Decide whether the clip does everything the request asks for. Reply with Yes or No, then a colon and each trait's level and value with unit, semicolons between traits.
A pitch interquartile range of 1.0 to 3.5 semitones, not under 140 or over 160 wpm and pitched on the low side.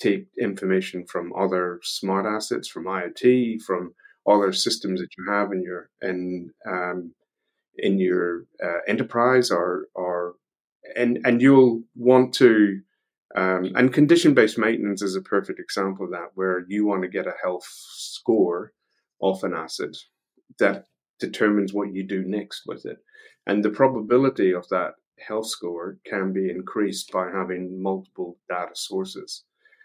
No: average, 4.5 semitones; average, 150 wpm; very low, 95 Hz